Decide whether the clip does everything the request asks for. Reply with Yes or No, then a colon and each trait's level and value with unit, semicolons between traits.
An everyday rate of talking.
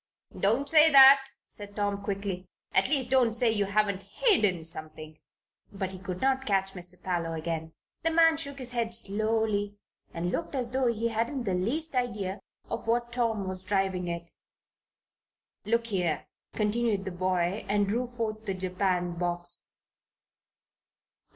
Yes: average, 150 wpm